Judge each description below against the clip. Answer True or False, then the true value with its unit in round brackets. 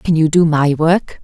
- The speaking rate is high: True (245 wpm)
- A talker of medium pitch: True (160 Hz)